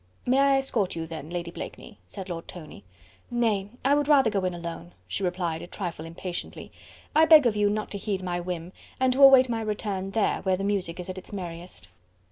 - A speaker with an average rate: No, fast, 215 wpm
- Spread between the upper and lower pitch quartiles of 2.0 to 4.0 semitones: No, average, 4.6 semitones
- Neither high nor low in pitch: No, high, 195 Hz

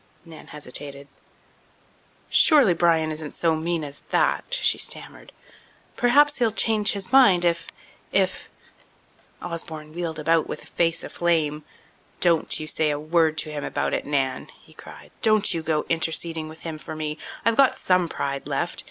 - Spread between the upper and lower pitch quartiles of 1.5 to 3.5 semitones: Yes, narrow, 2.5 semitones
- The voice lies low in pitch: No, medium, 165 Hz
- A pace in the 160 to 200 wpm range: No, average, 150 wpm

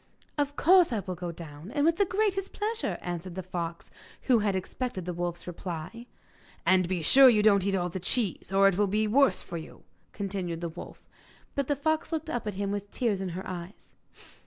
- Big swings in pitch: Yes, wide, 6.3 semitones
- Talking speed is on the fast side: Yes, fast, 210 wpm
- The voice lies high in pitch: Yes, high, 195 Hz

